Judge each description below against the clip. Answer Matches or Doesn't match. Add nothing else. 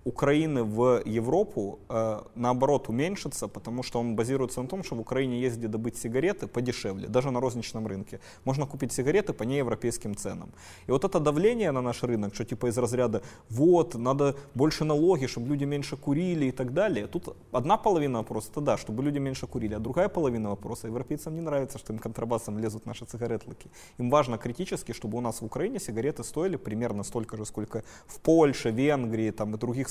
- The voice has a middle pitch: Doesn't match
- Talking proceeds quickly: Matches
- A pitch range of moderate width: Matches